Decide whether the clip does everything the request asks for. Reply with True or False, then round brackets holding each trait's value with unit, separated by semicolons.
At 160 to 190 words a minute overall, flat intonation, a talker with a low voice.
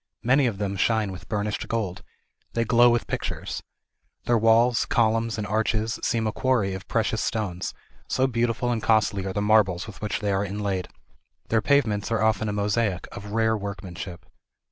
True (175 wpm; 2.2 semitones; 110 Hz)